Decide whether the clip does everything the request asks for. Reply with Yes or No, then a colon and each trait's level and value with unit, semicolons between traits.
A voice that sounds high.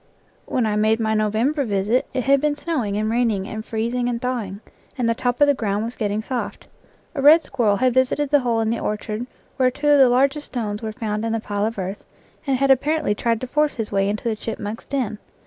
Yes: high, 230 Hz